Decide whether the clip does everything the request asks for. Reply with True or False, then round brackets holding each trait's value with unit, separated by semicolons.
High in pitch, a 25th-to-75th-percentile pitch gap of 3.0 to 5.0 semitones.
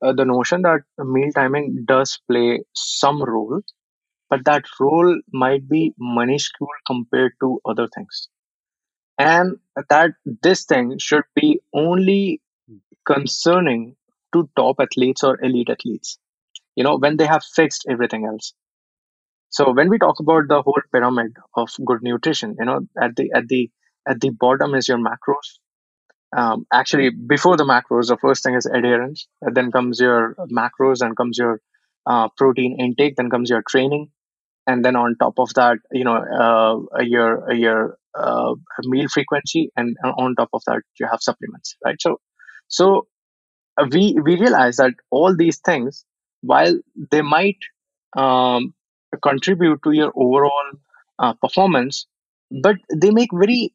False (135 Hz; 3.9 semitones)